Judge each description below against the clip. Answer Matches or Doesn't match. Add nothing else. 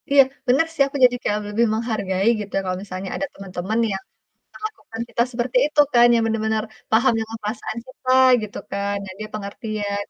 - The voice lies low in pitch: Doesn't match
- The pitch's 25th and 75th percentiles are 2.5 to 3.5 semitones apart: Matches